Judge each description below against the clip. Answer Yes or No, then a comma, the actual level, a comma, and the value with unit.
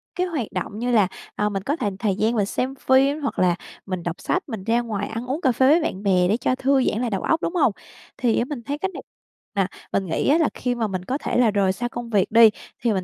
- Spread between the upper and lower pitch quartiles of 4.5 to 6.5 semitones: Yes, average, 5.1 semitones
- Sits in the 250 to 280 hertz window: No, high, 235 Hz